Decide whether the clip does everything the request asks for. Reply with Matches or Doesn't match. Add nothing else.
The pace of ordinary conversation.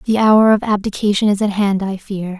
Doesn't match